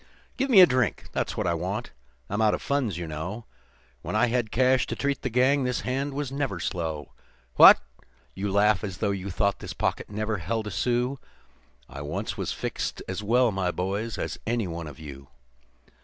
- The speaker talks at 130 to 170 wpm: No, average, 200 wpm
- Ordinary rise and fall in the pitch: No, wide, 5.7 semitones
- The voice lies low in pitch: Yes, low, 105 Hz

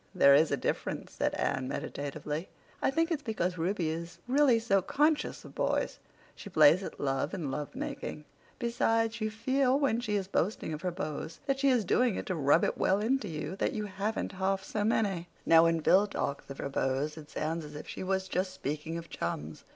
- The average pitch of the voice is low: No, medium, 185 Hz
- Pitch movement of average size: No, wide, 6.3 semitones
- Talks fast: Yes, fast, 210 wpm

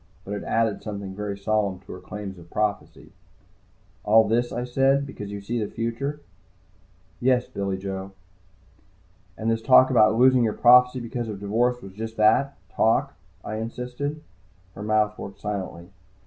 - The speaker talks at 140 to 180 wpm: Yes, average, 160 wpm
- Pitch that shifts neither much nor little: Yes, average, 3.5 semitones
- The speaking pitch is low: Yes, low, 110 Hz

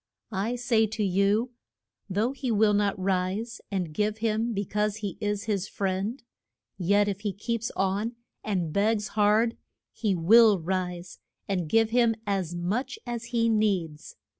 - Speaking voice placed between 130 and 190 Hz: No, high, 210 Hz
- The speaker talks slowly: No, average, 155 wpm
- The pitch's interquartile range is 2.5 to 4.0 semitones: Yes, average, 2.9 semitones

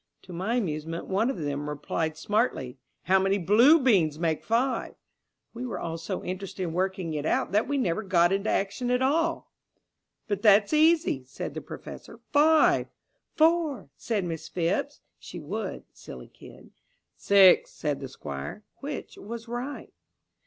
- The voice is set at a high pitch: Yes, high, 195 Hz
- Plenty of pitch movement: Yes, wide, 7.1 semitones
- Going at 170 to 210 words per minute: No, average, 155 wpm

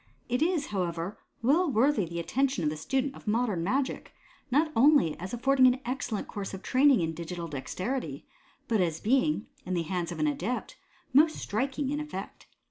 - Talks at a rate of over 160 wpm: Yes, average, 180 wpm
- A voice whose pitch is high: Yes, high, 240 Hz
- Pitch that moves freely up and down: Yes, wide, 7.3 semitones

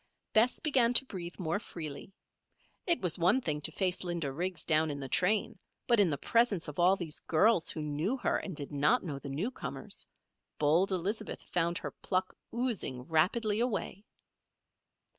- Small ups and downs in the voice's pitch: No, wide, 5.6 semitones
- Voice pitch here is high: No, medium, 180 Hz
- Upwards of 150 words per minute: Yes, average, 170 wpm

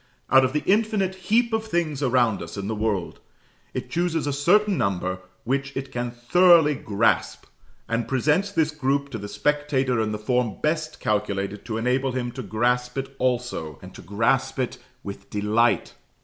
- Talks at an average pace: Yes, average, 175 wpm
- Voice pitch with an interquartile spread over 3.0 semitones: Yes, average, 5.3 semitones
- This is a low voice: Yes, low, 130 Hz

